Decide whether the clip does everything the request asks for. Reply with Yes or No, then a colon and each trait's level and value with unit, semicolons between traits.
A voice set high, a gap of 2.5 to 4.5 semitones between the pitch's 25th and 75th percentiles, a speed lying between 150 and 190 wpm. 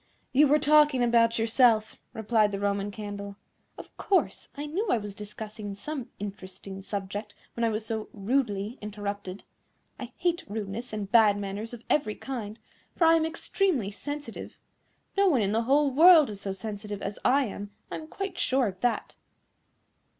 No: high, 220 Hz; average, 5.2 semitones; average, 170 wpm